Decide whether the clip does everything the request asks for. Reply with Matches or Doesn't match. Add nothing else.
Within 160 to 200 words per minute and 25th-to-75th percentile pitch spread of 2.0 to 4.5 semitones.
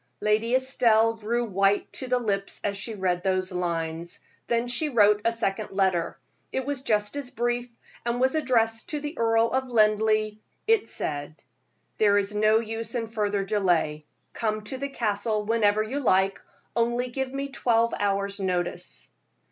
Matches